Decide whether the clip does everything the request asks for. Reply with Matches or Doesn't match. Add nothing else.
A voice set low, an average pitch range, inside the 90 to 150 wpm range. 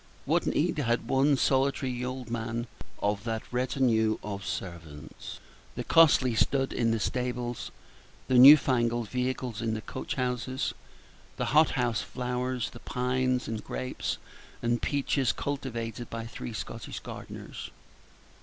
Doesn't match